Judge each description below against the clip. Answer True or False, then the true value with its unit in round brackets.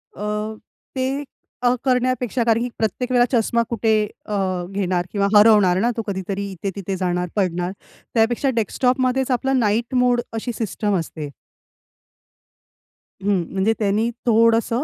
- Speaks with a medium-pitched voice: False (220 Hz)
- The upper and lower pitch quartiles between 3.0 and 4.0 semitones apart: True (3.6 semitones)